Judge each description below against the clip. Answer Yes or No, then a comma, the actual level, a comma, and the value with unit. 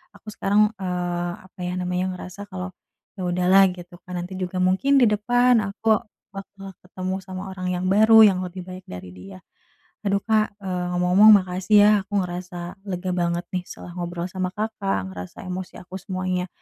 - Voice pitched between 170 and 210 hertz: Yes, medium, 185 Hz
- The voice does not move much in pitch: Yes, narrow, 1.7 semitones